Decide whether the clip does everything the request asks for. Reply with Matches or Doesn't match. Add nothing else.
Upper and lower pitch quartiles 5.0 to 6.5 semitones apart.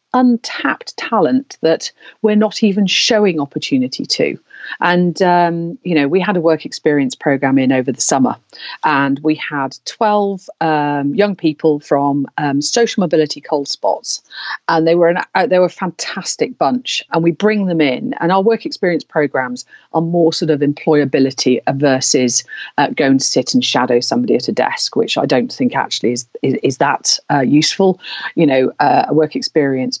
Matches